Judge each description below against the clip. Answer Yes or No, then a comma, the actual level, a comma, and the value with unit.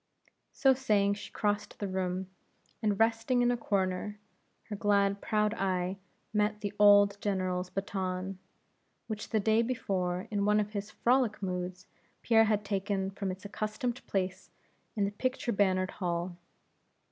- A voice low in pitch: No, high, 200 Hz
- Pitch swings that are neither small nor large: No, narrow, 2.1 semitones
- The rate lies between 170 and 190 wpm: No, average, 145 wpm